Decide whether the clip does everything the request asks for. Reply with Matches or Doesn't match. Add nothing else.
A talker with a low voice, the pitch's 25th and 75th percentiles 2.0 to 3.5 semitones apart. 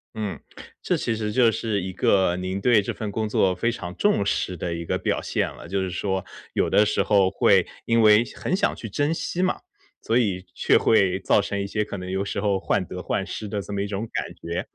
Matches